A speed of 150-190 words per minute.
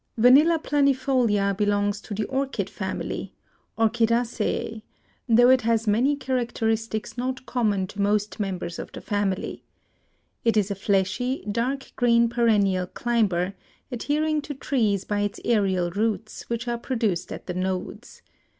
No: slow, 135 wpm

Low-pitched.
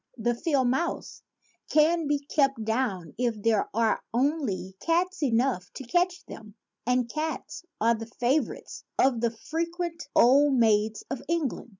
No: very high, 255 Hz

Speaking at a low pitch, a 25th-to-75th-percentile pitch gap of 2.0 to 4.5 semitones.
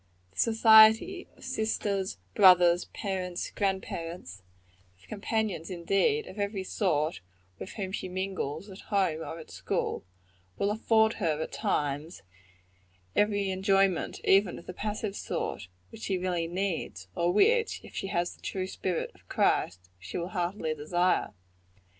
No: high, 190 Hz; average, 3.2 semitones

